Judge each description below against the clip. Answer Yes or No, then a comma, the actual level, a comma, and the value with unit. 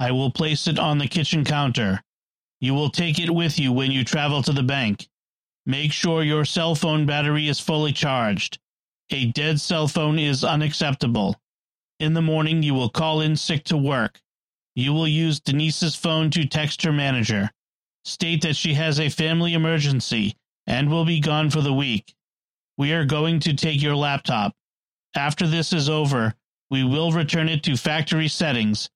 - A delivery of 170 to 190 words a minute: Yes, average, 180 wpm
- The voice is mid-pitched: Yes, medium, 150 Hz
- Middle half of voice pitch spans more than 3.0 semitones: No, narrow, 2.5 semitones